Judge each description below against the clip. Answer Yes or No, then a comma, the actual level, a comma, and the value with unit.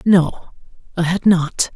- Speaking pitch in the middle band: Yes, medium, 175 Hz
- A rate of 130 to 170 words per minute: Yes, slow, 135 wpm